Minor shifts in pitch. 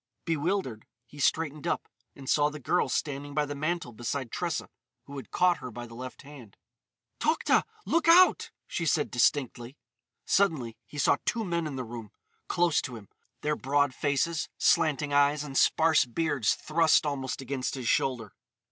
No: average, 3.9 semitones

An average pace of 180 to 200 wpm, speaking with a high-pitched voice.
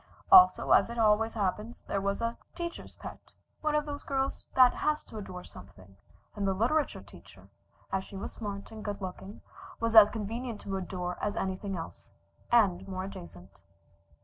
No: average, 170 wpm; high, 205 Hz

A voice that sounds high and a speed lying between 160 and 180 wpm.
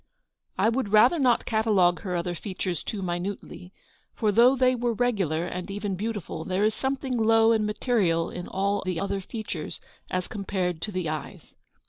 Yes: high, 200 Hz; average, 175 wpm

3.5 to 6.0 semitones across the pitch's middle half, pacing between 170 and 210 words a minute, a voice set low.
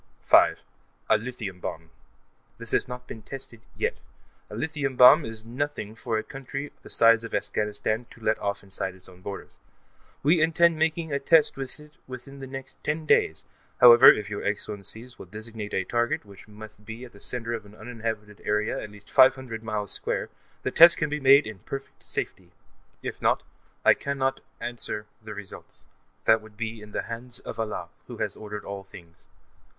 Yes: average, 4.2 semitones; average, 185 wpm; low, 115 Hz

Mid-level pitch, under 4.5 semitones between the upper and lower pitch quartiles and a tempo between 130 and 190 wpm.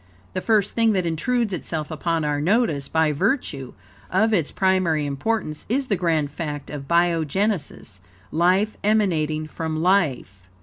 No: medium, 165 Hz; average, 4.9 semitones; average, 140 wpm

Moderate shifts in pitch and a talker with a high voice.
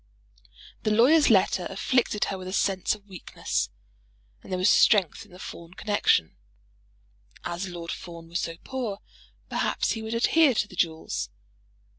Yes: average, 3.9 semitones; high, 195 Hz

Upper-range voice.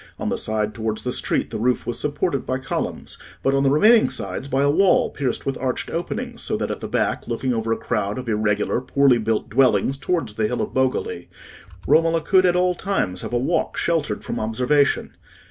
No: low, 130 Hz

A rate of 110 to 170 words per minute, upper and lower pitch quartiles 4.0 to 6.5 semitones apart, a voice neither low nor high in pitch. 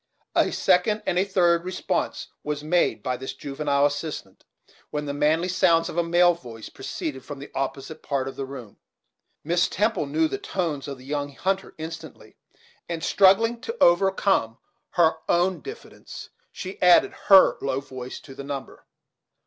Yes: average, 160 wpm; average, 4.6 semitones; medium, 160 Hz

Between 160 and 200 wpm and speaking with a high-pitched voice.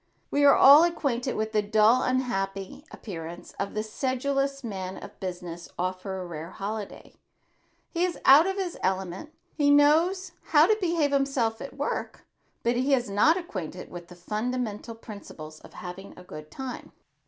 Yes: average, 165 wpm; high, 225 Hz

